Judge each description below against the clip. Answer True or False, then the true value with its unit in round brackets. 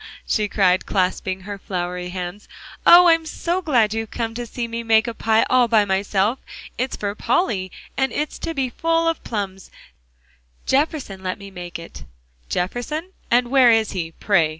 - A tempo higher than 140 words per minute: True (175 wpm)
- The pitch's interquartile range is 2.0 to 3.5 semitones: False (5.3 semitones)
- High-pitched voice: True (220 Hz)